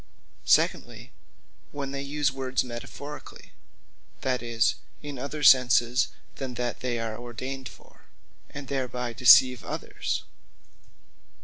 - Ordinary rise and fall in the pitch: No, narrow, 2.2 semitones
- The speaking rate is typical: No, slow, 110 wpm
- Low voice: Yes, low, 130 Hz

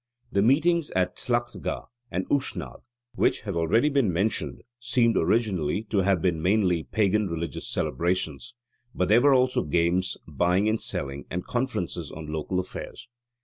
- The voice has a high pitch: No, very low, 95 Hz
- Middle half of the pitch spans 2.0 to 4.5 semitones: No, wide, 5.5 semitones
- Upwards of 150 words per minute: No, average, 145 wpm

